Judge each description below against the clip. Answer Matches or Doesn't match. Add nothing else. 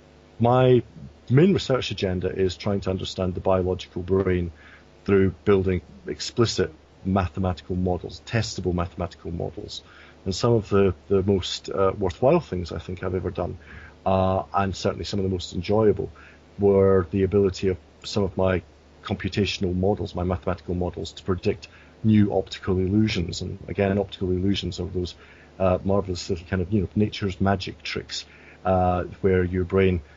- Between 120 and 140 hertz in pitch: Doesn't match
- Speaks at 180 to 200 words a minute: Doesn't match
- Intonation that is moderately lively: Doesn't match